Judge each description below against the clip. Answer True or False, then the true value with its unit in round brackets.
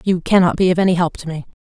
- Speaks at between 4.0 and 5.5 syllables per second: False (7.3 syllables/s)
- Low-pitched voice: False (175 Hz)